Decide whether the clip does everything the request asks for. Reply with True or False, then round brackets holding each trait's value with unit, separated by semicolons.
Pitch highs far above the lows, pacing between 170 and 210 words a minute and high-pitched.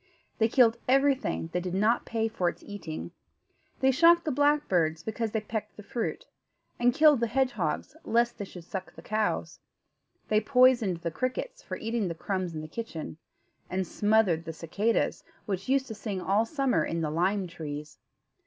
True (5.8 semitones; 175 wpm; 215 Hz)